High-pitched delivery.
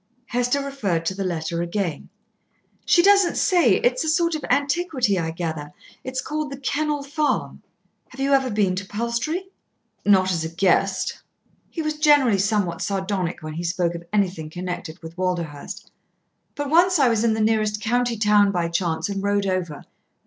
Yes: high, 205 Hz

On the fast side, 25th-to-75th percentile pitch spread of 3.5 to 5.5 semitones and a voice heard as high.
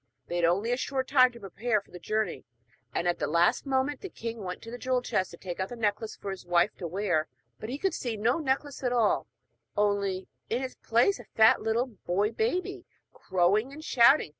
Yes: fast, 220 wpm; average, 5.2 semitones; high, 225 Hz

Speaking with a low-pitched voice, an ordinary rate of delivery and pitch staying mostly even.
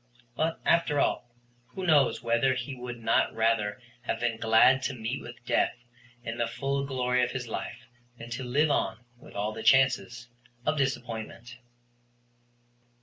Yes: low, 125 Hz; average, 155 wpm; narrow, 2.3 semitones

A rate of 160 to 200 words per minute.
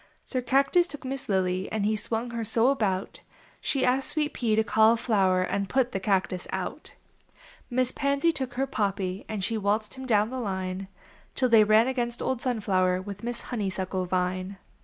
Yes: average, 180 wpm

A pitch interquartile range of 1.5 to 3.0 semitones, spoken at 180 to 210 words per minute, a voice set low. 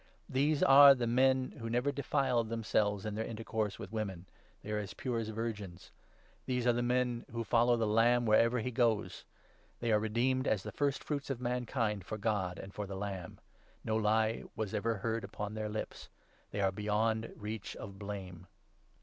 Yes: narrow, 2.6 semitones; average, 195 wpm; low, 110 Hz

